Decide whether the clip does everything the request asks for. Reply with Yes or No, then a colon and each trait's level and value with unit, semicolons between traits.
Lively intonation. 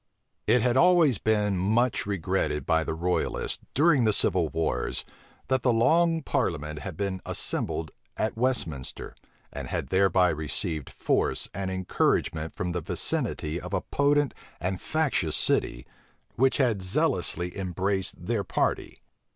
Yes: wide, 6.0 semitones